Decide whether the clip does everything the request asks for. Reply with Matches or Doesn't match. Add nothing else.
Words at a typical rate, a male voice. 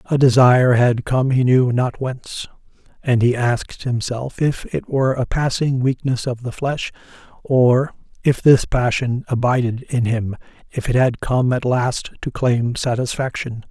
Matches